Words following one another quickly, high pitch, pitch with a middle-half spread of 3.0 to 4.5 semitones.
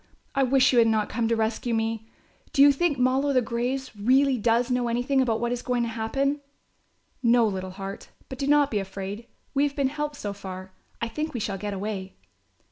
Yes: fast, 215 wpm; high, 235 Hz; average, 3.9 semitones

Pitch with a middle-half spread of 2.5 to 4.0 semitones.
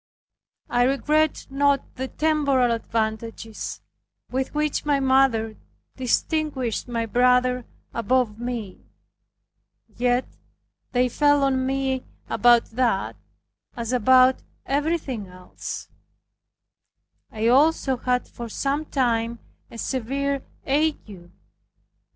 Yes: average, 3.0 semitones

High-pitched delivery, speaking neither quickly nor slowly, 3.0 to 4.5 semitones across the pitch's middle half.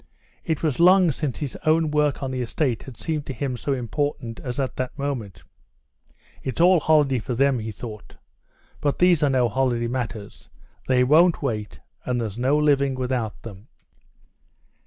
No: low, 130 Hz; average, 170 wpm; average, 3.6 semitones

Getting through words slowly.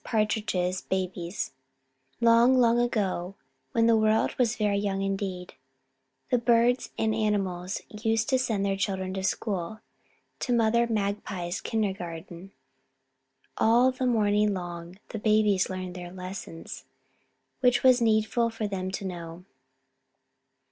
Yes: slow, 125 wpm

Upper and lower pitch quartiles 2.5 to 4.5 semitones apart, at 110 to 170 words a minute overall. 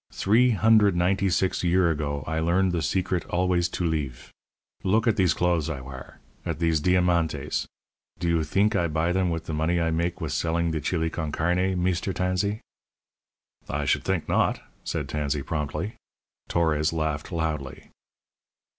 Yes: average, 2.8 semitones; average, 165 wpm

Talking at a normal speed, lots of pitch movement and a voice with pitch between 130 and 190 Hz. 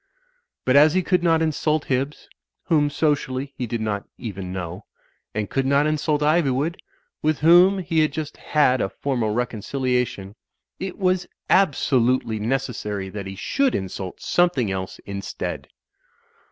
Yes: average, 150 wpm; wide, 6.4 semitones; low, 135 Hz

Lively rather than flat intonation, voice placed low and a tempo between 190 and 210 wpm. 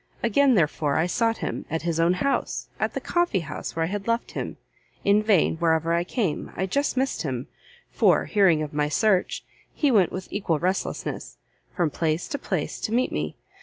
No: wide, 5.8 semitones; medium, 180 Hz; average, 195 wpm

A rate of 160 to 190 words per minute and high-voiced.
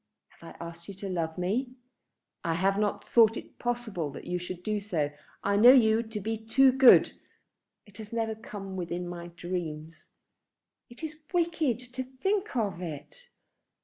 Yes: average, 170 wpm; high, 210 Hz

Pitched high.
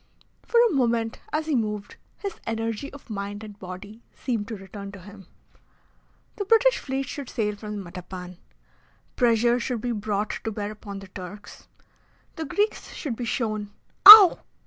Yes: high, 220 Hz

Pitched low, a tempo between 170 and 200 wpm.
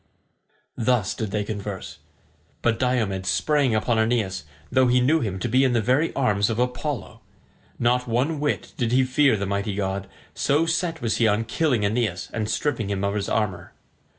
Yes: low, 115 Hz; average, 180 wpm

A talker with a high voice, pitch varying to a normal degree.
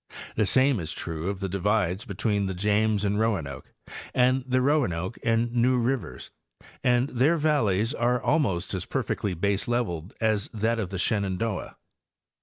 No: low, 105 Hz; average, 4.4 semitones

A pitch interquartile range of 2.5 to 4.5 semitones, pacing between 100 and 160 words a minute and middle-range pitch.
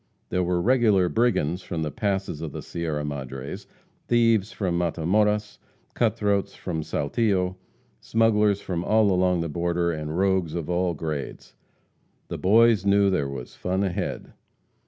No: average, 3.9 semitones; average, 145 wpm; very low, 90 Hz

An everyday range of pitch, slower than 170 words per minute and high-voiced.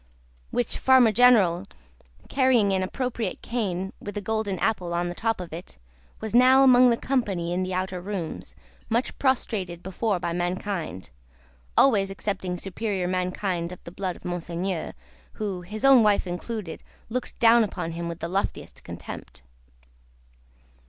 Yes: average, 4.2 semitones; average, 150 wpm; high, 195 Hz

